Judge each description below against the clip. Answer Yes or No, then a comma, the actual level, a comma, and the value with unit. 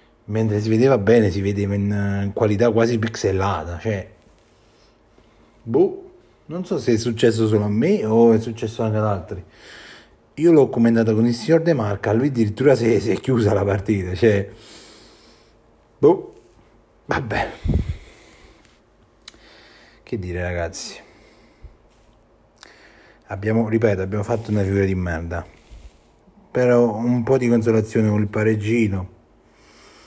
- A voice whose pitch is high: No, low, 110 Hz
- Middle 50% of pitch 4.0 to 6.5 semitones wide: No, average, 2.7 semitones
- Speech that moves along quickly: No, average, 125 wpm